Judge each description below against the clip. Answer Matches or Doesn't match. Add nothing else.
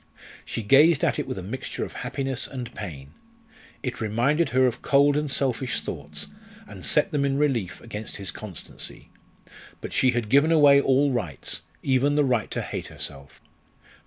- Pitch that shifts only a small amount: Doesn't match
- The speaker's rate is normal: Matches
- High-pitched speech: Doesn't match